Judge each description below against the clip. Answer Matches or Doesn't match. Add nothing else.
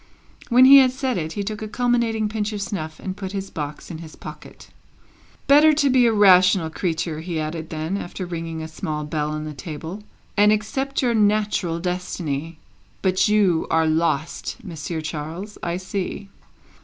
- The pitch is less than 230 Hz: Matches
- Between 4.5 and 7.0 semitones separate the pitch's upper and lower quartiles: Matches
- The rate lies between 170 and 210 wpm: Matches